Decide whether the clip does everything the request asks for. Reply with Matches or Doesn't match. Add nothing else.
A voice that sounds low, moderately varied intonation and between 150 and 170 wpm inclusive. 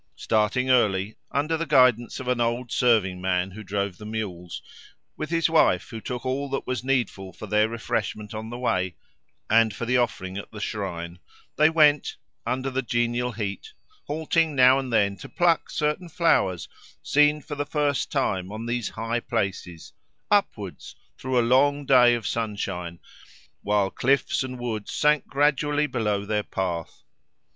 Matches